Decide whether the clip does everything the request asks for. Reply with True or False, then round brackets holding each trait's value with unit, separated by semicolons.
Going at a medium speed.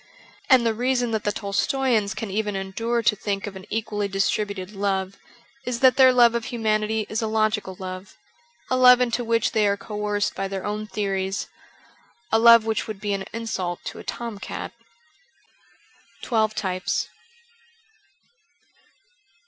True (155 wpm)